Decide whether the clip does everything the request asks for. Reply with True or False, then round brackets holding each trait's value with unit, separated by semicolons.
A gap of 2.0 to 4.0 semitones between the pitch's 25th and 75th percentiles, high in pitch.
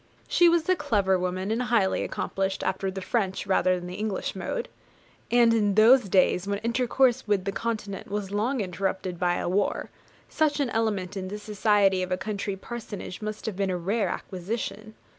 True (3.3 semitones; 205 Hz)